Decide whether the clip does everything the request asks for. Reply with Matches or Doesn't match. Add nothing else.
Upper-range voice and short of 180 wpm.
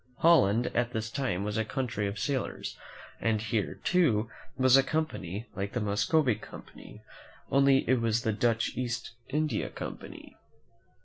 Doesn't match